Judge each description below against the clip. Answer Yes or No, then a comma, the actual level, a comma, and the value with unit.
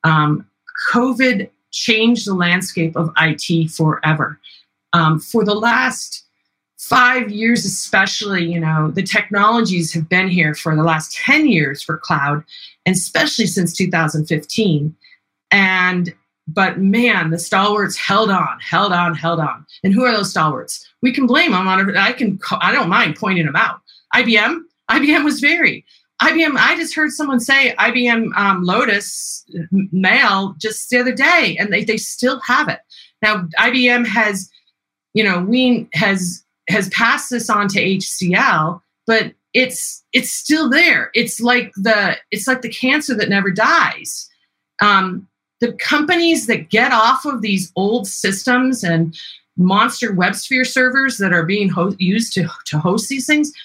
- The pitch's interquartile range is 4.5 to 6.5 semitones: Yes, wide, 5.6 semitones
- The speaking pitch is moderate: No, high, 205 Hz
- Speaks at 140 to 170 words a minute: Yes, average, 155 wpm